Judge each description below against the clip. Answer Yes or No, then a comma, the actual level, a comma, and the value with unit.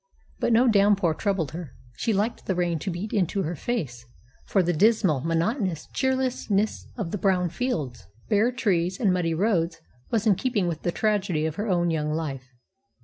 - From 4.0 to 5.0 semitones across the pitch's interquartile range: Yes, average, 4.6 semitones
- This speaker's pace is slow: No, average, 180 wpm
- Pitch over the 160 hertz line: Yes, medium, 185 Hz